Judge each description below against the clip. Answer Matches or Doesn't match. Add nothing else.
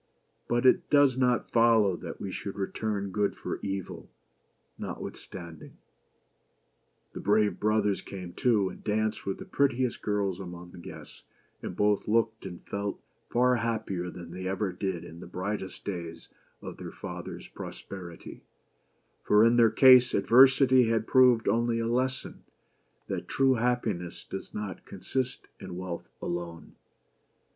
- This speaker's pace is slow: Doesn't match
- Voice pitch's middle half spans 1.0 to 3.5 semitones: Doesn't match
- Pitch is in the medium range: Doesn't match